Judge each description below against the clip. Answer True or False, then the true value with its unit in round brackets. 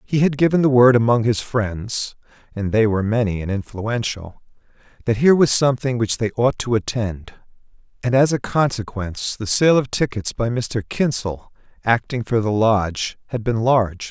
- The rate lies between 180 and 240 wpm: False (165 wpm)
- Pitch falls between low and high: False (115 Hz)